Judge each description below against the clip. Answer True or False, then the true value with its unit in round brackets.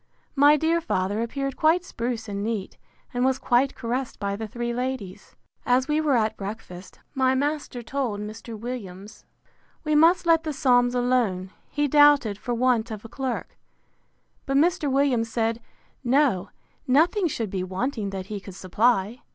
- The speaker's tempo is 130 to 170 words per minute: True (160 wpm)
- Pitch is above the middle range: True (245 Hz)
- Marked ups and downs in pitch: False (4.6 semitones)